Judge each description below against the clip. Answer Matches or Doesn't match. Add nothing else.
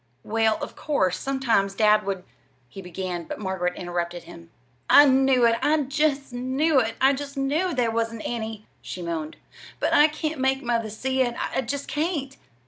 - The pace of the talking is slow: Doesn't match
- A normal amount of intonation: Doesn't match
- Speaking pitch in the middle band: Doesn't match